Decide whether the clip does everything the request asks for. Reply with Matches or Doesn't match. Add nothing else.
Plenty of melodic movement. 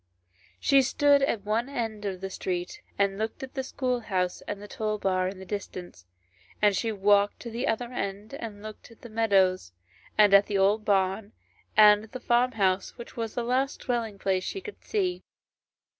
Doesn't match